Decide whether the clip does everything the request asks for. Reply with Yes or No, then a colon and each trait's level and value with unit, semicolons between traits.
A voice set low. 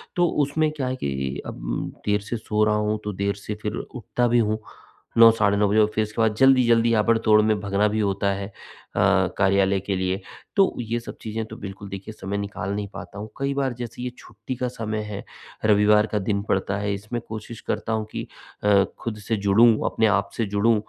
Yes: low, 105 Hz